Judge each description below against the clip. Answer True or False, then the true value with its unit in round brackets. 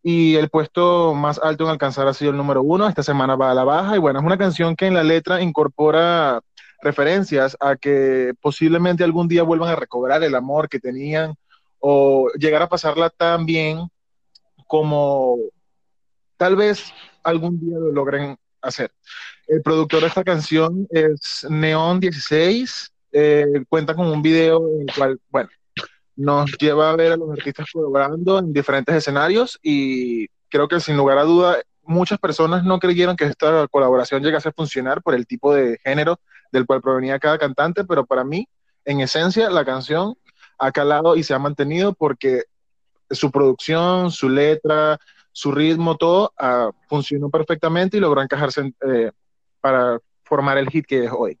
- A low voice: False (155 Hz)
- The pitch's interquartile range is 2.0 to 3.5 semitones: True (3.2 semitones)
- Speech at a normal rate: True (170 wpm)